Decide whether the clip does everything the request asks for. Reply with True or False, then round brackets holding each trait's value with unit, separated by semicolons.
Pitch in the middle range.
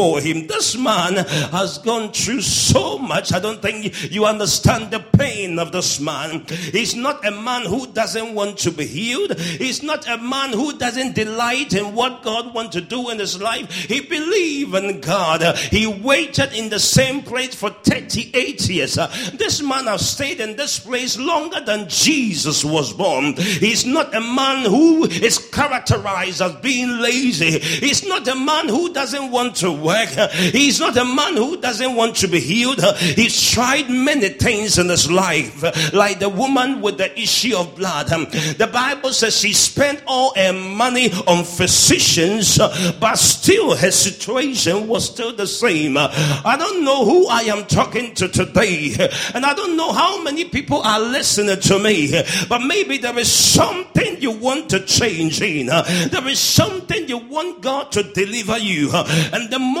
False (220 Hz)